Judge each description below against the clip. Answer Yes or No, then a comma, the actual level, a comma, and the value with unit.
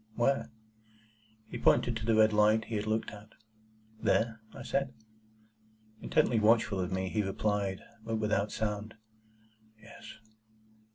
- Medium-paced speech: No, slow, 130 wpm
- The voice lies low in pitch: Yes, low, 110 Hz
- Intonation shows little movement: Yes, narrow, 1.4 semitones